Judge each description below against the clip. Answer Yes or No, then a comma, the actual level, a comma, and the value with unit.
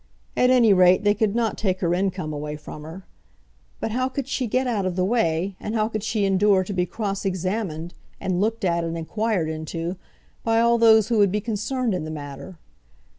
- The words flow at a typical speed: No, fast, 210 wpm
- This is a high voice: Yes, high, 195 Hz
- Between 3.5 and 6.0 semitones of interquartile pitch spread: Yes, average, 4.2 semitones